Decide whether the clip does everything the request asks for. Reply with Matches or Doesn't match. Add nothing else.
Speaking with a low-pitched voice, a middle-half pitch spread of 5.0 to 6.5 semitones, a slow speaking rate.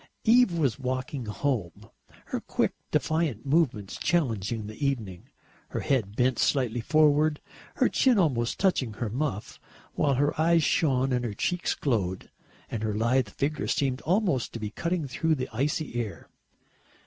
Doesn't match